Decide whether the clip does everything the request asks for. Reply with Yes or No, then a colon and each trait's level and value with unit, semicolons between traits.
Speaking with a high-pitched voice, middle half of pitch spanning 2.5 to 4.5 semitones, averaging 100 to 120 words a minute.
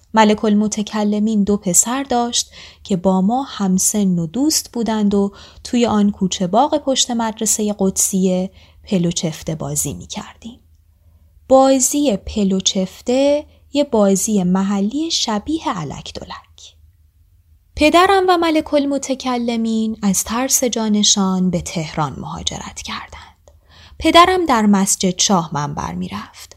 No: high, 205 Hz; average, 5.3 semitones; average, 115 wpm